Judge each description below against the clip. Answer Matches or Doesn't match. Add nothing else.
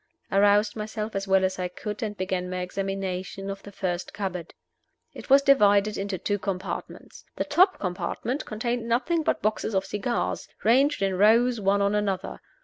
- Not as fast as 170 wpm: Doesn't match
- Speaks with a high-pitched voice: Matches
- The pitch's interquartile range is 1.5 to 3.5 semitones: Matches